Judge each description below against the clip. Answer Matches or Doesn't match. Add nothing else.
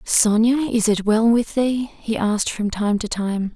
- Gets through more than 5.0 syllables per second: Doesn't match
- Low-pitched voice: Doesn't match